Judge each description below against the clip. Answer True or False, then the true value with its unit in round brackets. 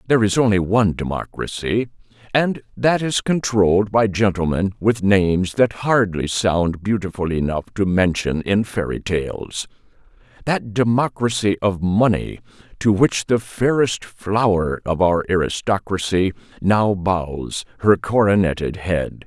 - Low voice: True (100 Hz)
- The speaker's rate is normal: False (120 wpm)